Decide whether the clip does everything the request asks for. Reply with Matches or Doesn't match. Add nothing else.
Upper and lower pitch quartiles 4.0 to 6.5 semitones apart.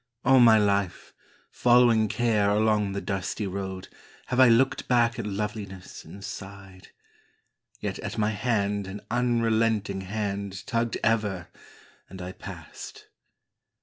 Doesn't match